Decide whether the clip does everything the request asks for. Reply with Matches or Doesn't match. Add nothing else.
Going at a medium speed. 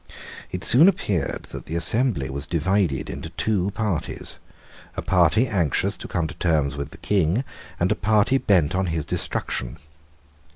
Matches